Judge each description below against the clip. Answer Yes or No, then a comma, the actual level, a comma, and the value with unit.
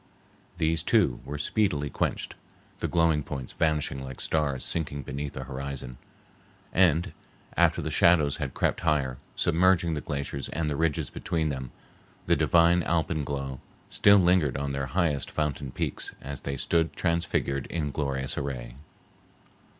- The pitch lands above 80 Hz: No, very low, 75 Hz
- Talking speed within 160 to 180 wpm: No, average, 140 wpm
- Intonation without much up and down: No, average, 3.2 semitones